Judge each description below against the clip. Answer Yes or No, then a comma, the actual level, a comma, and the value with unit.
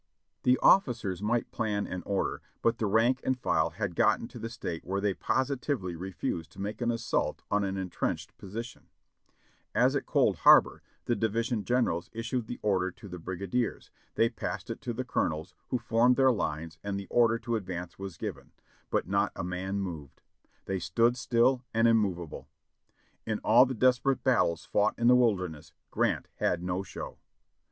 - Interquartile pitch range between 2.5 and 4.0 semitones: No, average, 4.5 semitones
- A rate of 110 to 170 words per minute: No, average, 180 wpm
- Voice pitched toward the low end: Yes, low, 105 Hz